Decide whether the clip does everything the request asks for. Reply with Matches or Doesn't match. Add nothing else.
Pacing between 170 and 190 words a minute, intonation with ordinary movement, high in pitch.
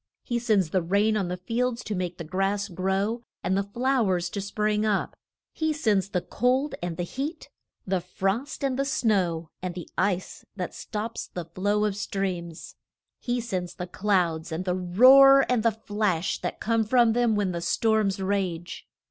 Matches